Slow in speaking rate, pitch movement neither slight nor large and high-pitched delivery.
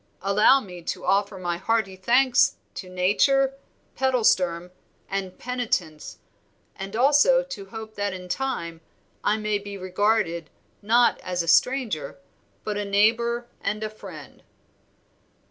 Yes: slow, 130 wpm; average, 4.6 semitones; high, 205 Hz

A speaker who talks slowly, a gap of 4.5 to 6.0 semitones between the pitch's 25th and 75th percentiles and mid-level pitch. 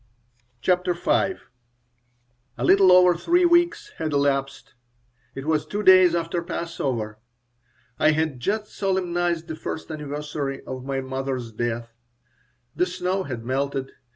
Yes: slow, 125 wpm; average, 5.2 semitones; medium, 160 Hz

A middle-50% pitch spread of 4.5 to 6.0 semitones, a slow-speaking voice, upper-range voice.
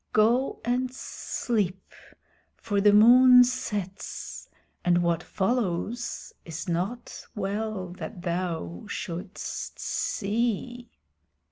Yes: average, 4.9 semitones; slow, 95 wpm; high, 205 Hz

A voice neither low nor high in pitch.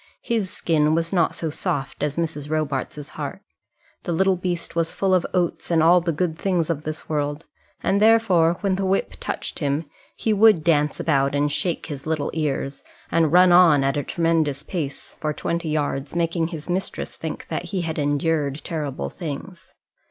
Yes: medium, 165 Hz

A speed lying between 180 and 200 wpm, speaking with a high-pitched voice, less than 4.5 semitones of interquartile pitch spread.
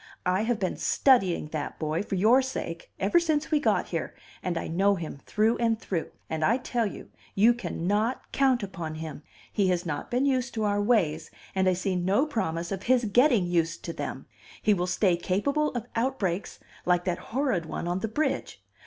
No: average, 195 wpm; high, 200 Hz; wide, 5.6 semitones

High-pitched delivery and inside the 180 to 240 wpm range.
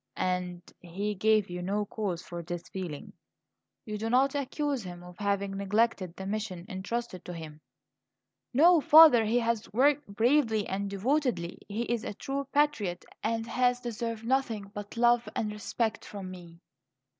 No: high, 210 Hz; average, 155 wpm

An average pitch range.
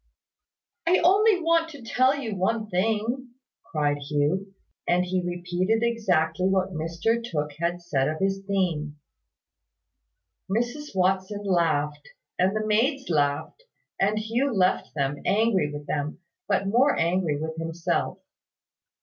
No: wide, 5.9 semitones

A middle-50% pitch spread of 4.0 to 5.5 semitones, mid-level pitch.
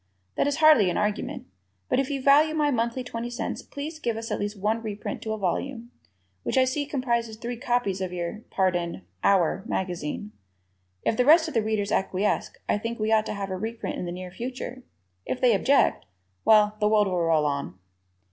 No: average, 4.6 semitones; high, 220 Hz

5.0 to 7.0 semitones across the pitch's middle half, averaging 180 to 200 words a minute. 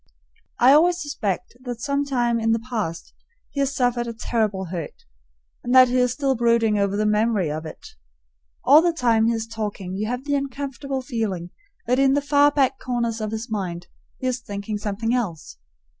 No: average, 3.9 semitones; average, 190 wpm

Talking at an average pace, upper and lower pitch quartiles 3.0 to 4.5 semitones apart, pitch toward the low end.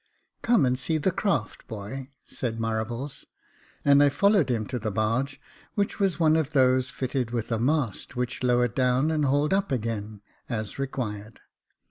Yes: average, 170 wpm; average, 4.1 semitones; low, 130 Hz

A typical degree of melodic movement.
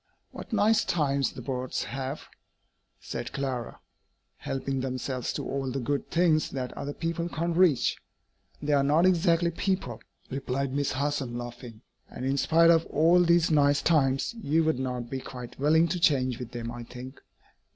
Yes: average, 4.2 semitones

